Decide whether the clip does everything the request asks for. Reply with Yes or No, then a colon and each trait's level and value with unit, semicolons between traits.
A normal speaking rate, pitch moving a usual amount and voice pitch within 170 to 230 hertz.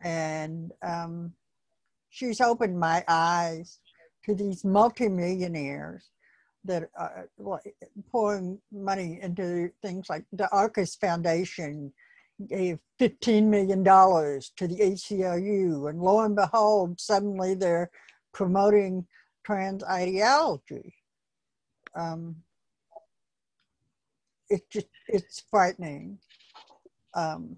No: slow, 85 wpm; average, 3.3 semitones; medium, 185 Hz